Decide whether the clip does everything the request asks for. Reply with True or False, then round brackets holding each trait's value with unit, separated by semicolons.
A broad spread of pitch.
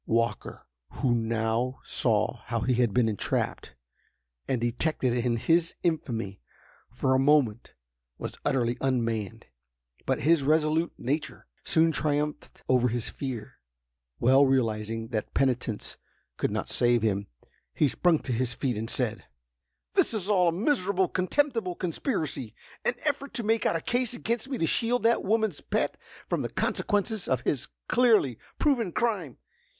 True (7.8 semitones)